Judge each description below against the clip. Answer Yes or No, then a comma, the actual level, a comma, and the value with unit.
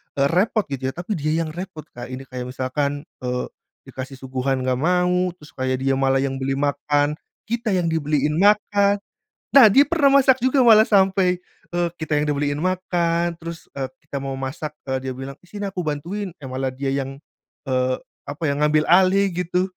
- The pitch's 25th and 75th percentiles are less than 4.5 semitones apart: No, average, 5.3 semitones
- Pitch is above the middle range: No, medium, 150 Hz